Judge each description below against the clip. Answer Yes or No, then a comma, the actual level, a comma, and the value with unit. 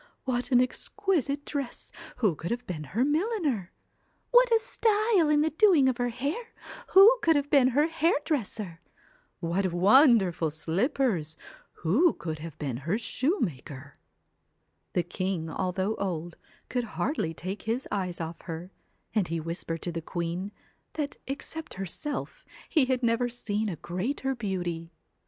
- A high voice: Yes, high, 225 Hz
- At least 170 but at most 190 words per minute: No, average, 145 wpm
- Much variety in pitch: Yes, wide, 8.8 semitones